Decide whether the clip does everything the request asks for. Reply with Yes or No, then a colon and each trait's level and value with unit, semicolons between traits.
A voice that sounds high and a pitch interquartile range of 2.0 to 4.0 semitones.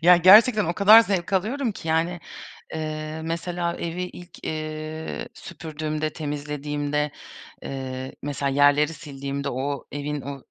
No: medium, 155 Hz; average, 3.2 semitones